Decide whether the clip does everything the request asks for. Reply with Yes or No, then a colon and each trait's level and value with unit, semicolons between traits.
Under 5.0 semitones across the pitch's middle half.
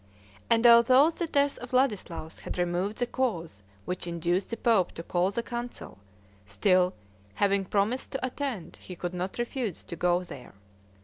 No: wide, 5.5 semitones